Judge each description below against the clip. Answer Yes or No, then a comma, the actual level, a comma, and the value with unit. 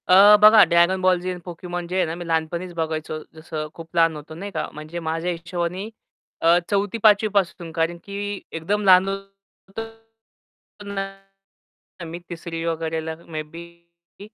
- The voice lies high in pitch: No, medium, 175 Hz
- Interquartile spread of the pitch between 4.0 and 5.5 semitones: No, average, 3.0 semitones